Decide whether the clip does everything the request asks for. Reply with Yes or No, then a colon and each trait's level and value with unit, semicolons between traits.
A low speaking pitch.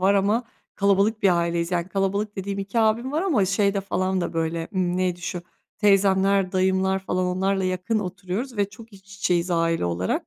No: high, 190 Hz